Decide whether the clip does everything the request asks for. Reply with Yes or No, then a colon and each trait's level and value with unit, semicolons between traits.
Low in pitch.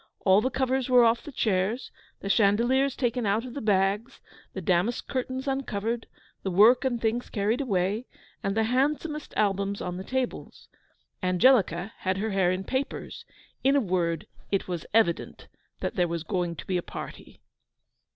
No: high, 215 Hz